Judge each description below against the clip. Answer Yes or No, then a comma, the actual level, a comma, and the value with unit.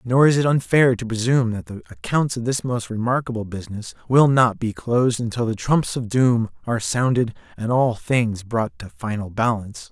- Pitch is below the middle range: Yes, low, 115 Hz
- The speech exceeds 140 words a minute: Yes, average, 195 wpm